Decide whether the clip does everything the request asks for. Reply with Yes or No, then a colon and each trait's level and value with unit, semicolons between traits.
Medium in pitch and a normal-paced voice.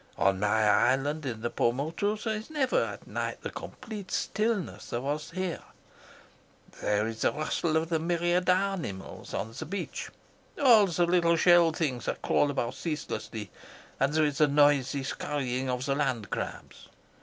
Yes: medium, 150 Hz; average, 165 wpm